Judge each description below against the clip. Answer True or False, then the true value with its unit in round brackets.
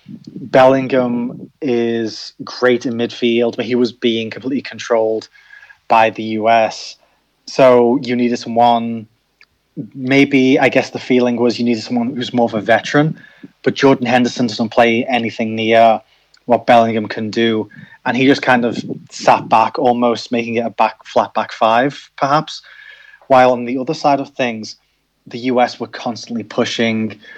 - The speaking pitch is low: True (120 Hz)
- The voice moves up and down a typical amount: False (2.2 semitones)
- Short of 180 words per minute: True (155 wpm)